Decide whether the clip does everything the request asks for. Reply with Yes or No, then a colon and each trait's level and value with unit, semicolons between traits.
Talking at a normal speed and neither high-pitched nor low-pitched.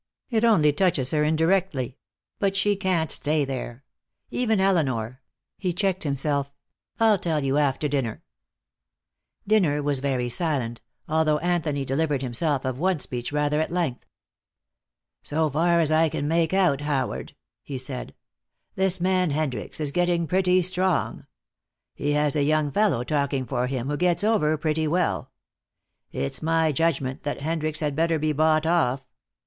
Yes: average, 155 wpm; medium, 155 Hz